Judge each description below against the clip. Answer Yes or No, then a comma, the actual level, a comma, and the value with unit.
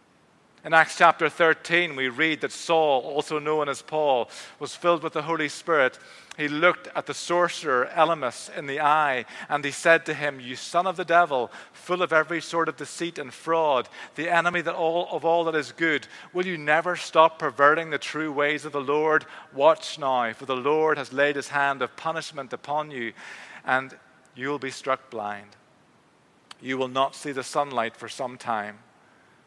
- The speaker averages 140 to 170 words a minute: No, average, 190 wpm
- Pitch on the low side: No, medium, 155 Hz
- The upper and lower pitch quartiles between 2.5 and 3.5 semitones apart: Yes, average, 3.2 semitones